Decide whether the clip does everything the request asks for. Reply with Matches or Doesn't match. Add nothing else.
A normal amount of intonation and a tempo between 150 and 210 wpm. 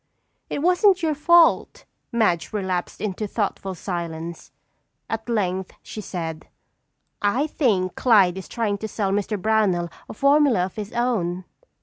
Doesn't match